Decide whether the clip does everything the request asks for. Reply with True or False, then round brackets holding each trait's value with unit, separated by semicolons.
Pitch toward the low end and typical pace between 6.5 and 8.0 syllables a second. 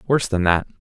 True (105 Hz; 7.1 syllables/s)